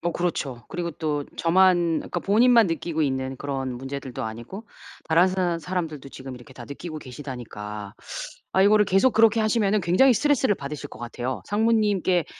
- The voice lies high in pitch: No, medium, 170 Hz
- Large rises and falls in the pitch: Yes, wide, 6.7 semitones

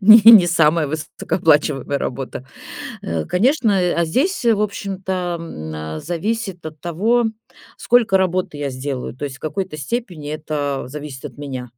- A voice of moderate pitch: Yes, medium, 165 Hz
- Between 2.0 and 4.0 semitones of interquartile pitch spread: No, average, 5.3 semitones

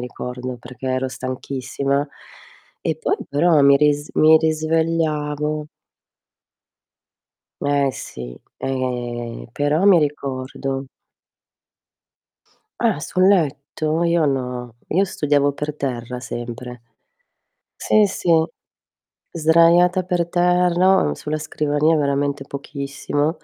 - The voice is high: No, medium, 145 Hz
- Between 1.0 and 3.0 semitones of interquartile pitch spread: No, average, 3.7 semitones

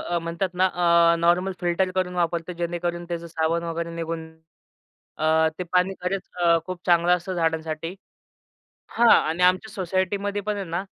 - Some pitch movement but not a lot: No, narrow, 1.7 semitones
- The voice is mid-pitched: Yes, medium, 175 Hz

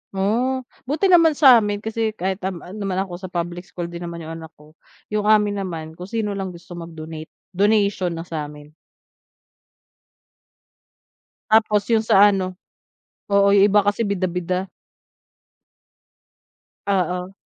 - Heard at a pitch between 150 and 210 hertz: Yes, high, 190 Hz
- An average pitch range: Yes, average, 3.3 semitones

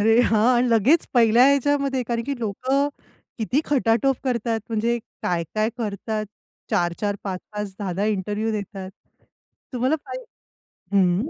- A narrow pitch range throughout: No, average, 3.6 semitones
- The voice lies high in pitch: Yes, high, 225 Hz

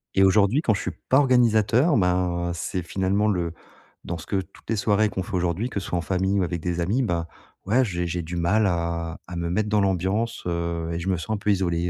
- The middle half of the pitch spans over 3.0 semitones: Yes, average, 3.5 semitones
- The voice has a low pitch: Yes, very low, 95 Hz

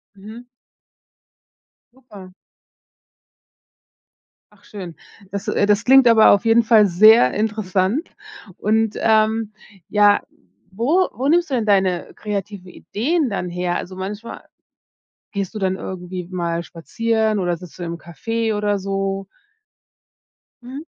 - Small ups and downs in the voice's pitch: No, average, 3.3 semitones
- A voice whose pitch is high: Yes, high, 205 Hz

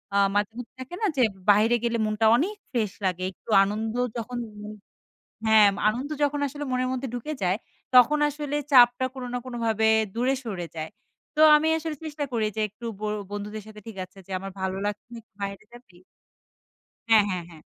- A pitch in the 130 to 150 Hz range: No, high, 225 Hz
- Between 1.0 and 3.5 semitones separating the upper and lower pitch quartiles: No, average, 4.0 semitones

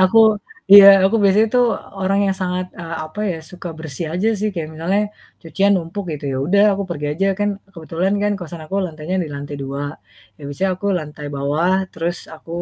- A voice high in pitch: No, medium, 175 Hz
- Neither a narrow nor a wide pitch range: Yes, average, 3.8 semitones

